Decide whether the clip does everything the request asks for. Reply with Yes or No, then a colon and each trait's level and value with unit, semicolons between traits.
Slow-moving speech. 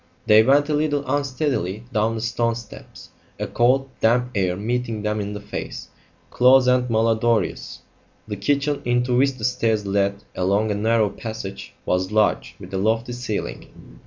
No: average, 165 wpm